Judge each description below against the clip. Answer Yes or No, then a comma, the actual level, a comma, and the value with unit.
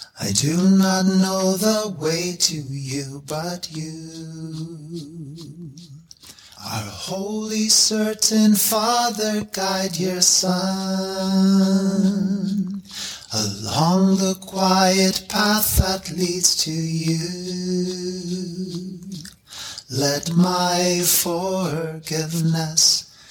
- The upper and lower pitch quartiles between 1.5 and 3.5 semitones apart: Yes, average, 3.0 semitones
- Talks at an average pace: No, slow, 70 wpm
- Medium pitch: Yes, medium, 180 Hz